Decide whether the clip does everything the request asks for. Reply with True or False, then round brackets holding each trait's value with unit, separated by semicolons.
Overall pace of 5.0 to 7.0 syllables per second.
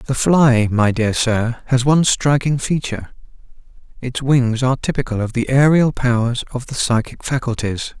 False (4.8 syllables/s)